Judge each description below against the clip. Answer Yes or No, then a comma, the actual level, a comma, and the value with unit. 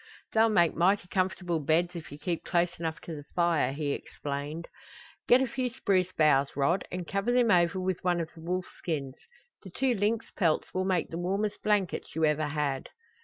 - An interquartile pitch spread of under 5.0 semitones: Yes, average, 3.5 semitones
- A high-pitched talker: No, medium, 175 Hz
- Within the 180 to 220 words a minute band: Yes, average, 195 wpm